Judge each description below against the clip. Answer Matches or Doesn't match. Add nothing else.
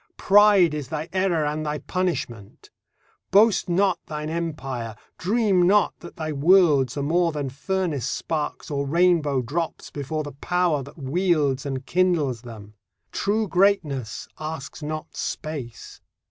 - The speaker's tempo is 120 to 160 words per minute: Matches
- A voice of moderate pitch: Matches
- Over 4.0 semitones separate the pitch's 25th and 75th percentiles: Matches